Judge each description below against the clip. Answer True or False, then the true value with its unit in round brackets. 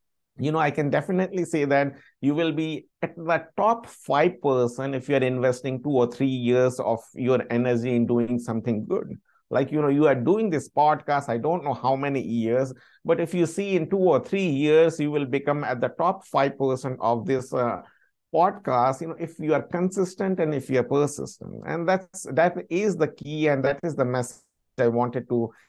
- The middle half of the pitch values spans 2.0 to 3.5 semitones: False (4.5 semitones)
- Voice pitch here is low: False (145 Hz)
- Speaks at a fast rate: True (210 wpm)